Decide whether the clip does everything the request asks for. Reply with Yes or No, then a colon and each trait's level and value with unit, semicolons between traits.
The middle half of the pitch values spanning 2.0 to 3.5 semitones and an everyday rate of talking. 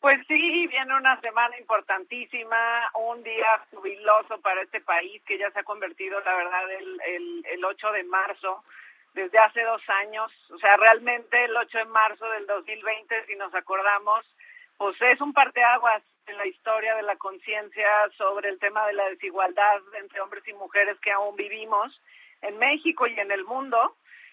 Yes: average, 2.7 semitones; average, 170 wpm